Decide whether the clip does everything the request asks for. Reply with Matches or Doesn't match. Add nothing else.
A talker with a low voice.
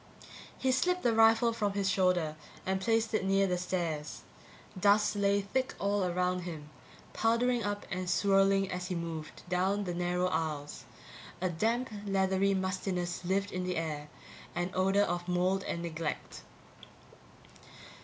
Doesn't match